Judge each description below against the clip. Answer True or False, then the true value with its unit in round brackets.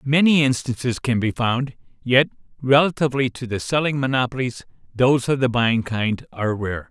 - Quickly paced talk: False (155 wpm)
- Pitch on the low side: True (125 Hz)